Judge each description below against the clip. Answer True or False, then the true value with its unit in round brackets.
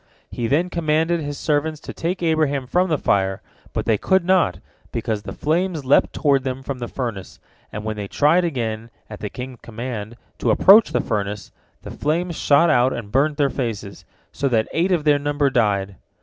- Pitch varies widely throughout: True (6.0 semitones)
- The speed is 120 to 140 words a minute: False (190 wpm)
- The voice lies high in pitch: False (140 Hz)